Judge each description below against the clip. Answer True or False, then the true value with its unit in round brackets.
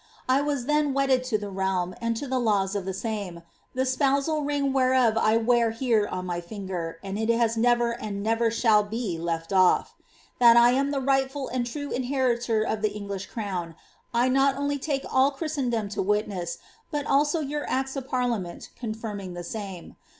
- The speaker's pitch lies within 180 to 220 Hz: False (235 Hz)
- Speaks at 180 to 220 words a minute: True (190 wpm)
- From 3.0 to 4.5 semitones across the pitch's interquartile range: False (4.9 semitones)